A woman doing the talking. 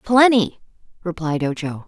Yes: female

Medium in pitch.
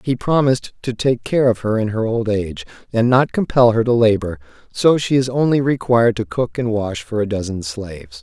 No: low, 110 Hz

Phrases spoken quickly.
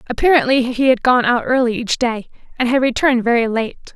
No: average, 195 wpm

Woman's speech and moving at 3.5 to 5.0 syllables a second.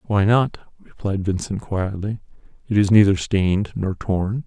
No: male; 4.5 syllables/s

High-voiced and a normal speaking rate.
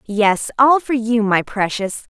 Yes: high, 225 Hz; average, 170 wpm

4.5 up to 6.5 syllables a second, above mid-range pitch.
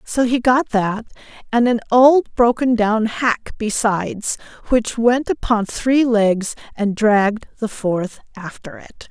No: 3.7 syllables/s; high, 225 Hz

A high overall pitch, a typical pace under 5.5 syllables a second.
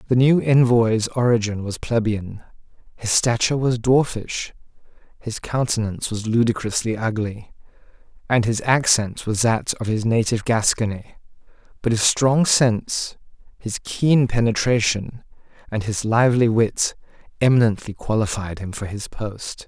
No: low, 115 Hz; 4.6 syllables/s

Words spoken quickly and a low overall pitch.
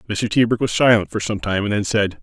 Yes: fast, 270 wpm; low, 105 Hz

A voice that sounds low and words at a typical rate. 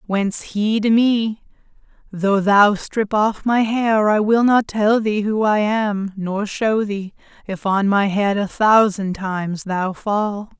No: high, 210 Hz; average, 170 wpm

